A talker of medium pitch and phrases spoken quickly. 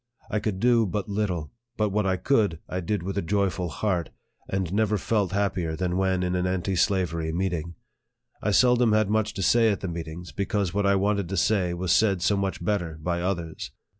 No: very low, 95 Hz; fast, 210 wpm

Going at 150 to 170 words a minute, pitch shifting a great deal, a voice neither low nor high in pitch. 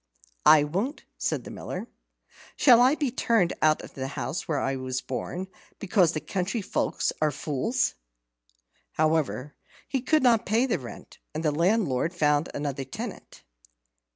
Yes: average, 155 wpm; wide, 7.7 semitones; medium, 165 Hz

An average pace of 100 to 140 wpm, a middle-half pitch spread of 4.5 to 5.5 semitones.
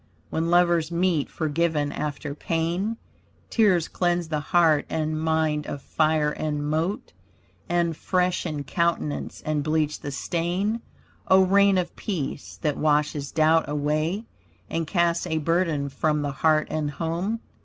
No: slow, 135 wpm; narrow, 2.5 semitones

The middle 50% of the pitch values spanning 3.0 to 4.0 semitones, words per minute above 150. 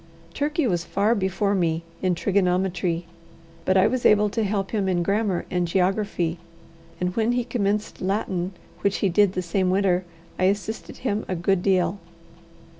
No: narrow, 2.4 semitones; average, 165 wpm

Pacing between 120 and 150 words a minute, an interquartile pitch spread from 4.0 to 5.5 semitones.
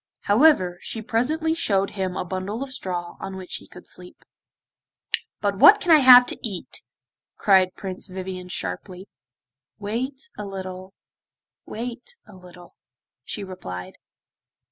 Yes: slow, 135 wpm; average, 5.0 semitones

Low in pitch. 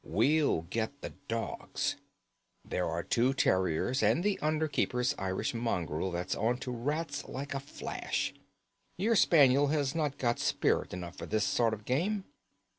Yes: low, 125 Hz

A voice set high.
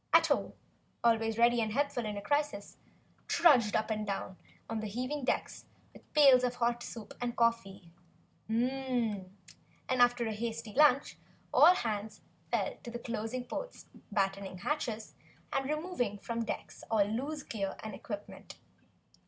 Yes: high, 230 Hz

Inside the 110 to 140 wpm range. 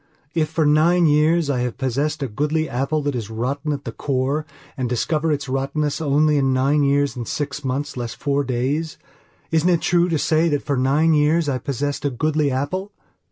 No: average, 200 wpm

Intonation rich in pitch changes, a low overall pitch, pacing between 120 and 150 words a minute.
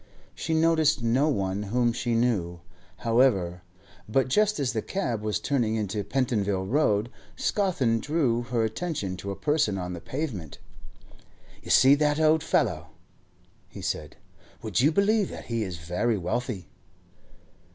Yes: wide, 6.6 semitones; low, 120 Hz; average, 145 wpm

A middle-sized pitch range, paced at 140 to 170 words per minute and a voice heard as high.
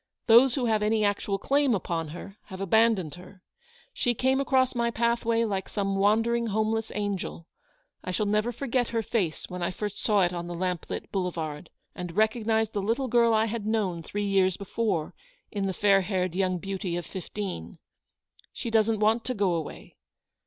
No: average, 3.5 semitones; average, 180 wpm; high, 205 Hz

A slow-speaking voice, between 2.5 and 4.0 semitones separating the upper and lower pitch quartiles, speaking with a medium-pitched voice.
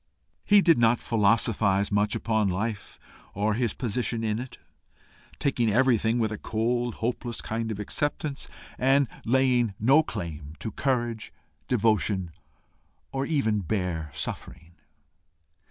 No: slow, 120 wpm; average, 3.3 semitones; low, 115 Hz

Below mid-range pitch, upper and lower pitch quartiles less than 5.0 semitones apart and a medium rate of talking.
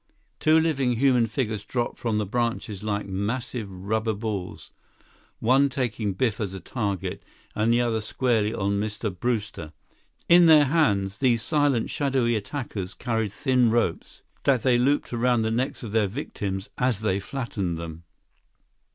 Yes: low, 115 Hz; average, 3.9 semitones; average, 150 wpm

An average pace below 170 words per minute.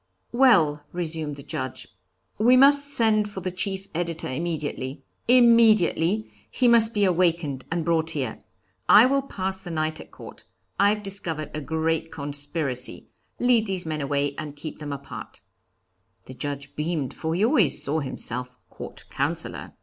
Yes: average, 150 wpm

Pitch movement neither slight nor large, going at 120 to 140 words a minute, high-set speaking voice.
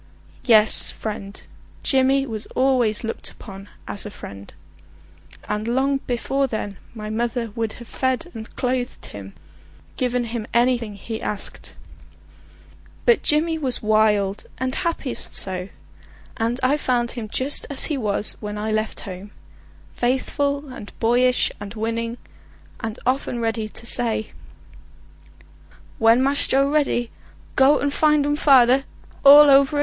Yes: average, 3.7 semitones; slow, 135 wpm; high, 240 Hz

